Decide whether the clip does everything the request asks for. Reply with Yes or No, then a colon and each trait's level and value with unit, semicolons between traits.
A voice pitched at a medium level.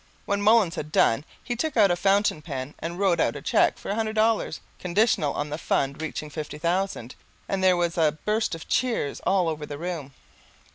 Yes: medium, 175 Hz